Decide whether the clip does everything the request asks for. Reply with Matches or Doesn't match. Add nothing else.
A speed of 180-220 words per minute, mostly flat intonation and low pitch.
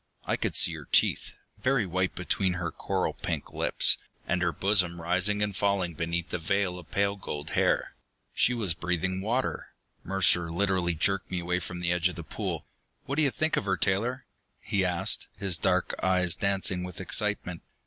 Matches